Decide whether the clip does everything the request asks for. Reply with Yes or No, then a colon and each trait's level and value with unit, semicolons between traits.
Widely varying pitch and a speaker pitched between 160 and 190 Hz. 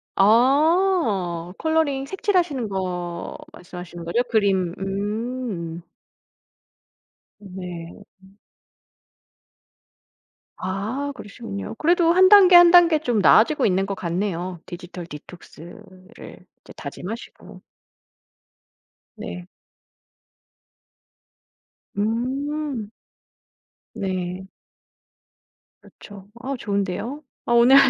No: wide, 7.2 semitones; high, 205 Hz